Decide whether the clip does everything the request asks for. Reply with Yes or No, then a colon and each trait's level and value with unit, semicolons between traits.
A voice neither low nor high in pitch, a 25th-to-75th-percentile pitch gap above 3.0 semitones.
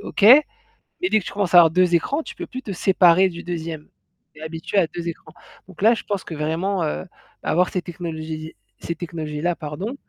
Yes: medium, 175 Hz; average, 3.4 semitones